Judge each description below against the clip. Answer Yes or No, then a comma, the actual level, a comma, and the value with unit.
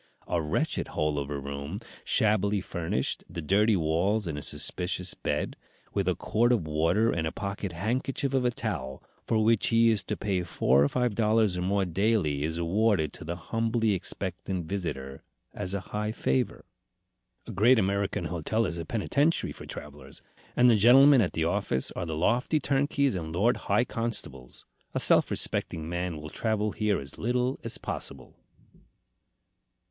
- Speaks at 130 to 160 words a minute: No, average, 170 wpm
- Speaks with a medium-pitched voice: No, low, 100 Hz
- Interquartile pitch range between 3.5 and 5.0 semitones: No, wide, 5.6 semitones